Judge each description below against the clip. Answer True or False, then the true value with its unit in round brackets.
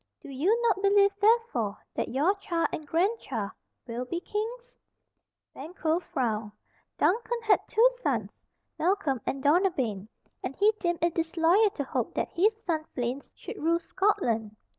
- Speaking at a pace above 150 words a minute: False (145 wpm)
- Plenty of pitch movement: True (7.3 semitones)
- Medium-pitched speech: False (335 Hz)